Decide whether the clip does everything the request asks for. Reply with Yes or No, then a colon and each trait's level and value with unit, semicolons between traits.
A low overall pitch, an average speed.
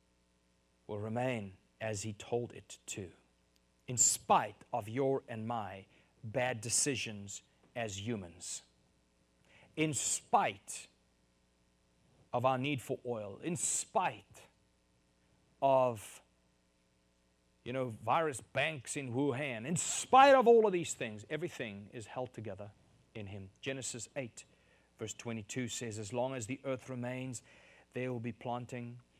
No: low, 115 Hz; slow, 125 wpm